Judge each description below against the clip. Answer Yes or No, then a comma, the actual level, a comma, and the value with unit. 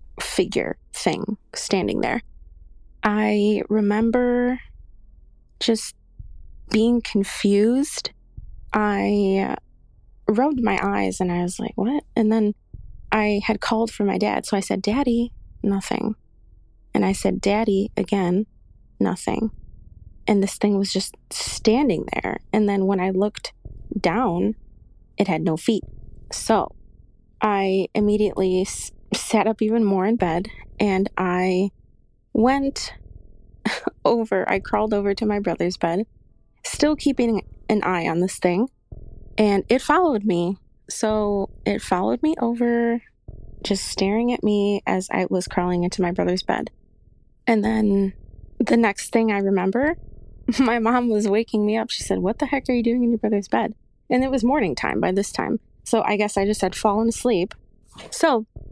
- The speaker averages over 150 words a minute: No, average, 145 wpm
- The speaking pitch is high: Yes, high, 210 Hz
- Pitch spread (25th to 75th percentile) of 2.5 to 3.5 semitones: Yes, average, 3.1 semitones